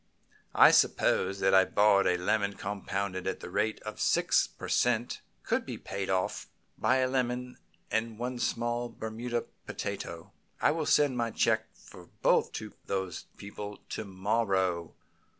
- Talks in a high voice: No, low, 105 Hz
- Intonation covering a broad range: No, average, 3.6 semitones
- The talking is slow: No, average, 150 wpm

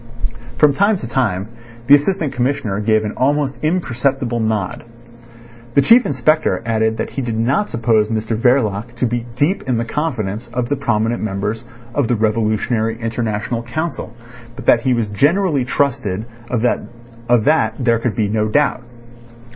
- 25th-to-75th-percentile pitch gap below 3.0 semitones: No, average, 3.9 semitones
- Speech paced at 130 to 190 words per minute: Yes, average, 155 wpm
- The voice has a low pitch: Yes, low, 120 Hz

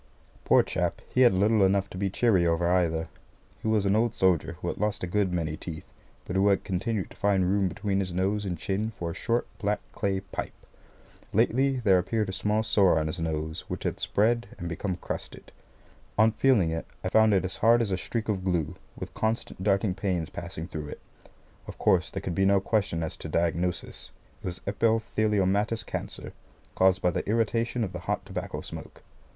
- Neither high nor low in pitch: No, very low, 95 Hz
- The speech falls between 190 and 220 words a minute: Yes, average, 200 wpm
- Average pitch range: Yes, average, 3.2 semitones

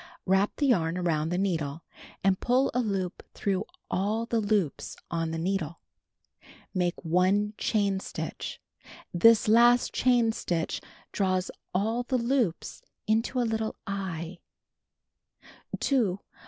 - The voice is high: Yes, high, 195 Hz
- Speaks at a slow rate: Yes, slow, 120 wpm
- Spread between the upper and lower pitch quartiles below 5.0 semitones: Yes, average, 4.2 semitones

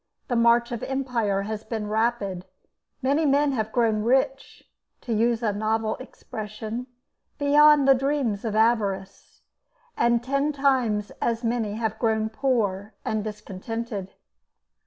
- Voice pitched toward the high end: Yes, high, 230 Hz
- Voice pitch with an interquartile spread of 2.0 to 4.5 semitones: Yes, average, 3.2 semitones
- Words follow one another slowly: Yes, slow, 130 wpm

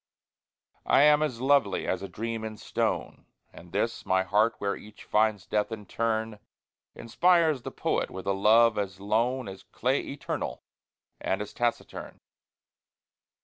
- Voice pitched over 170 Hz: No, low, 110 Hz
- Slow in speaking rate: No, average, 145 wpm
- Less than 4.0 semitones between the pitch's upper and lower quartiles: Yes, average, 3.1 semitones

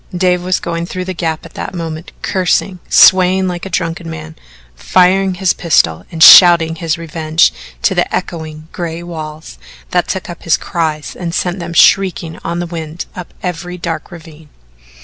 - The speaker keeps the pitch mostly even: Yes, narrow, 1.9 semitones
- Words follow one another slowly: No, average, 170 wpm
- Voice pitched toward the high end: No, medium, 170 Hz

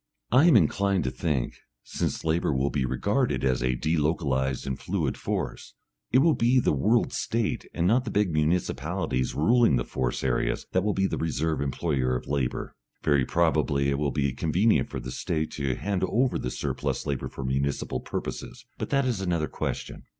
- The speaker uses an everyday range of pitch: No, wide, 6.5 semitones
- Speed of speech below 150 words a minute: No, average, 185 wpm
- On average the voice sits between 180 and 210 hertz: No, very low, 75 Hz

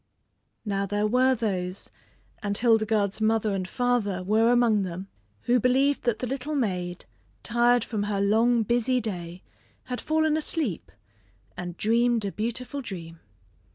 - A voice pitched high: Yes, high, 220 Hz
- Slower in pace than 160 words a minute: Yes, average, 140 wpm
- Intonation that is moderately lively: Yes, average, 3.7 semitones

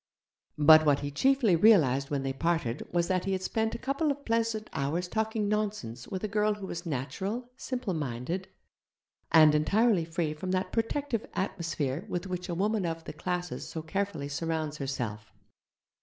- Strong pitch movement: Yes, wide, 5.9 semitones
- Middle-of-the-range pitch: Yes, medium, 175 Hz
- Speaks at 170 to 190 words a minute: Yes, average, 175 wpm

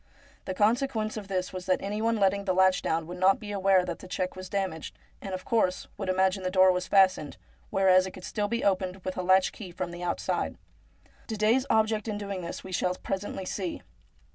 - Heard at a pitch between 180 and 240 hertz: Yes, high, 190 Hz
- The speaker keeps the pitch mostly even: Yes, narrow, 1.9 semitones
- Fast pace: Yes, fast, 220 wpm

